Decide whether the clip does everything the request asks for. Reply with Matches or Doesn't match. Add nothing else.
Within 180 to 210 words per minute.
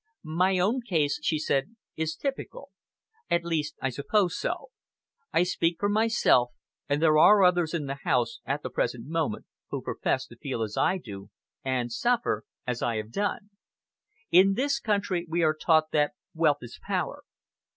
Doesn't match